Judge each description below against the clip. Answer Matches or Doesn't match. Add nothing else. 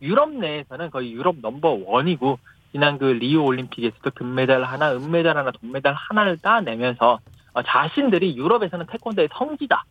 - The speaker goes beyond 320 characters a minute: Matches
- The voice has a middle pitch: Matches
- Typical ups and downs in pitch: Doesn't match